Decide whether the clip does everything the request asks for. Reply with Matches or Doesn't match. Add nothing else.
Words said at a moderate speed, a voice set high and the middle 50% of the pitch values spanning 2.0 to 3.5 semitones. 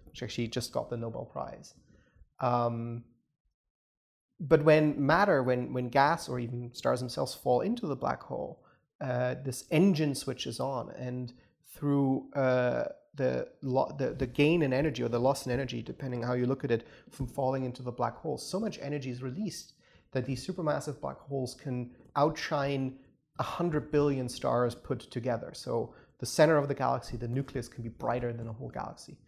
Doesn't match